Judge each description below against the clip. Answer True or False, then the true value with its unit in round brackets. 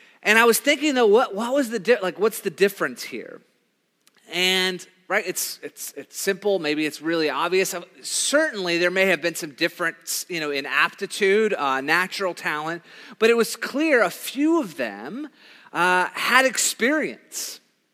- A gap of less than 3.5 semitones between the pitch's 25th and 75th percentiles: False (5.2 semitones)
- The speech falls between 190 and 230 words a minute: False (165 wpm)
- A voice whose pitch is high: True (195 Hz)